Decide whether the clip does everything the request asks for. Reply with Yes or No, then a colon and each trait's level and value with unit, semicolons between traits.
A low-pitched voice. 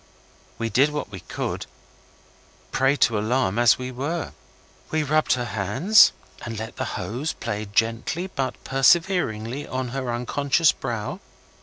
Yes: low, 130 Hz